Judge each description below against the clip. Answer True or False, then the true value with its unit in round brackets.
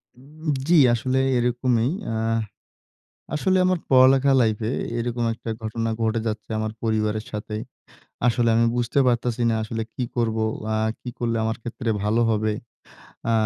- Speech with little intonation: True (2.2 semitones)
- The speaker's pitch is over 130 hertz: False (115 Hz)